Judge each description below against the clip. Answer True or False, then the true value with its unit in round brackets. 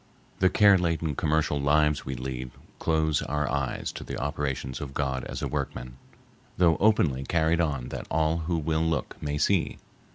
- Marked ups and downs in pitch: False (3.2 semitones)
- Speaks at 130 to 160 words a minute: False (170 wpm)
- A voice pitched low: True (75 Hz)